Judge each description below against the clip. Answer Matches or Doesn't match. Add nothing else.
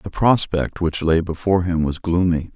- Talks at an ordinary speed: Matches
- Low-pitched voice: Matches